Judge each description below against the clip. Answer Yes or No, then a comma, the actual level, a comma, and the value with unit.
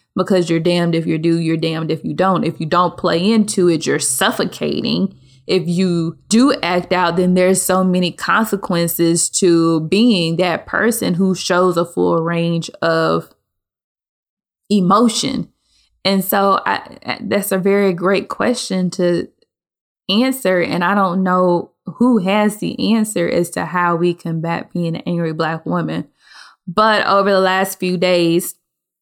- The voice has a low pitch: No, medium, 180 Hz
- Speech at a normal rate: Yes, average, 155 wpm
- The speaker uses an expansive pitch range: No, narrow, 2.5 semitones